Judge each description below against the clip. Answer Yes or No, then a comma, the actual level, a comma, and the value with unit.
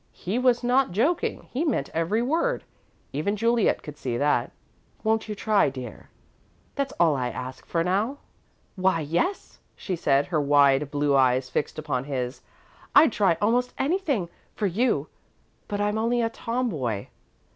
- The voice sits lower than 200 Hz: Yes, high, 190 Hz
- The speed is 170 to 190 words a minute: No, average, 155 wpm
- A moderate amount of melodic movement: No, wide, 8.8 semitones